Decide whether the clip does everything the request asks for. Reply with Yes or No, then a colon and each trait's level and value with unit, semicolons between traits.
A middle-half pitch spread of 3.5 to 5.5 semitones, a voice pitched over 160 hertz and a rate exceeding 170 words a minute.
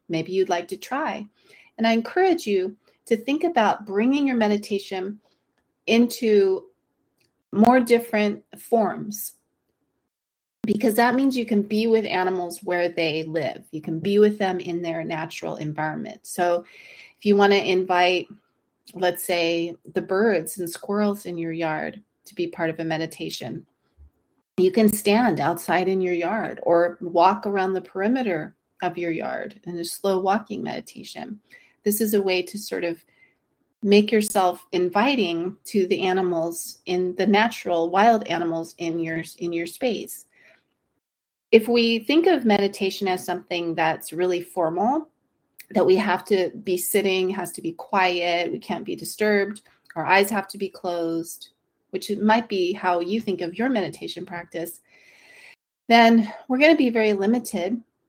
No: average, 4.0 semitones; high, 190 Hz; average, 155 wpm